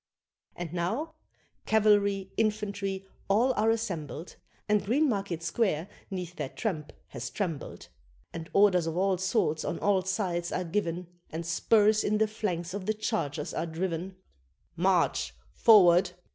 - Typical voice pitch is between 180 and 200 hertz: Yes, high, 190 Hz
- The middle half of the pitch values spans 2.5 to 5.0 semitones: Yes, average, 3.7 semitones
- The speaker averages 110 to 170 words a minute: Yes, slow, 135 wpm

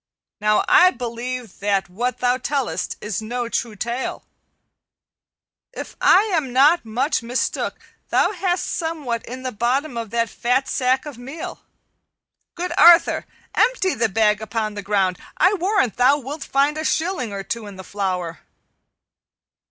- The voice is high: Yes, high, 245 Hz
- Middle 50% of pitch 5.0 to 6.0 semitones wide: Yes, wide, 5.5 semitones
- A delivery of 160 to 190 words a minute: No, average, 150 wpm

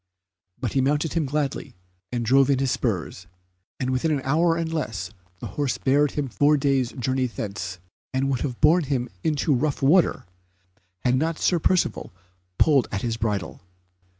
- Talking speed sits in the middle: Yes, average, 175 wpm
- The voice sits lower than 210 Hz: Yes, low, 135 Hz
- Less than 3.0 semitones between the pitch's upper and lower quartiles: No, average, 3.5 semitones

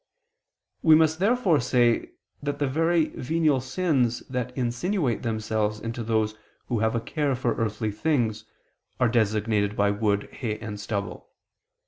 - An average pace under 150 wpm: Yes, average, 140 wpm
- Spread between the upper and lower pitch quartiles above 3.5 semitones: Yes, average, 5.0 semitones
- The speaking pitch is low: Yes, low, 120 Hz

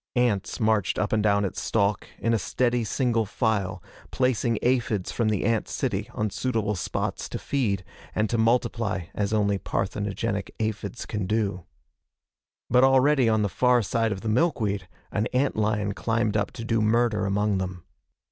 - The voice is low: Yes, low, 110 Hz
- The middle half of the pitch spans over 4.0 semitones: No, narrow, 2.5 semitones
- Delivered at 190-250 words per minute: No, average, 165 wpm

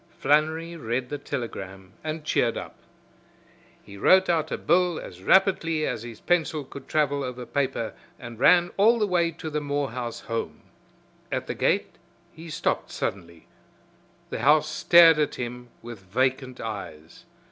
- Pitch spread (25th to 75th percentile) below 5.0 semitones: No, wide, 5.6 semitones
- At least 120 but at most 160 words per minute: Yes, average, 150 wpm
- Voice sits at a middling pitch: Yes, medium, 145 Hz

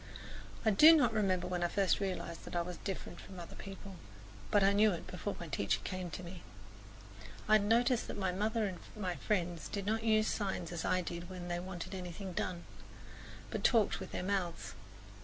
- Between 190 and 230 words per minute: Yes, average, 200 wpm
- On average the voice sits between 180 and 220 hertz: Yes, medium, 185 Hz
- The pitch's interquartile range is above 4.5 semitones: No, average, 2.8 semitones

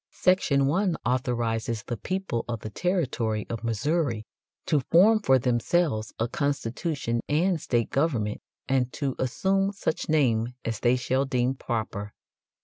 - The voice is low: Yes, low, 130 Hz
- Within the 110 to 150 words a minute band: Yes, average, 140 wpm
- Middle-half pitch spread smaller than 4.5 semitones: No, wide, 5.5 semitones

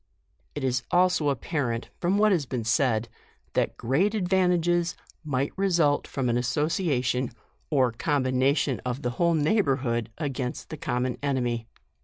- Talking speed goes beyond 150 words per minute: No, average, 140 wpm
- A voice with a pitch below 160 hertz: Yes, medium, 140 Hz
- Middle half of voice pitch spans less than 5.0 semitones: No, average, 5.3 semitones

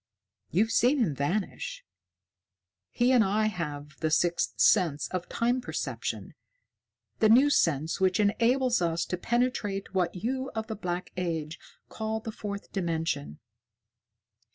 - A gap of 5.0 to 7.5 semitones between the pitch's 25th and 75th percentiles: Yes, wide, 5.4 semitones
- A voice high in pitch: Yes, high, 195 Hz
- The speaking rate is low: Yes, slow, 130 wpm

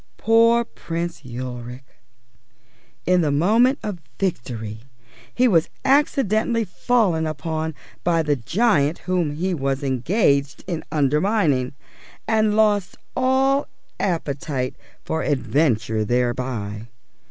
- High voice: No, medium, 160 Hz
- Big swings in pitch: Yes, wide, 8.1 semitones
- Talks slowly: Yes, slow, 100 wpm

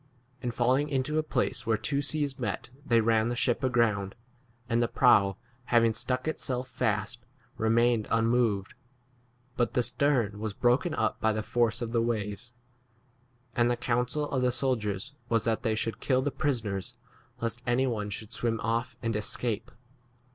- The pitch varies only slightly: Yes, narrow, 2.3 semitones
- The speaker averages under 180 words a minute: Yes, average, 170 wpm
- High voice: No, low, 120 Hz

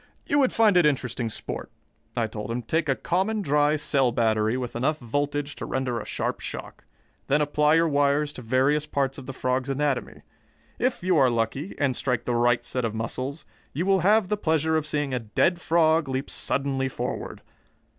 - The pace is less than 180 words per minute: No, average, 195 wpm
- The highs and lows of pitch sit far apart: No, average, 4.0 semitones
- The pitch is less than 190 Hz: Yes, medium, 140 Hz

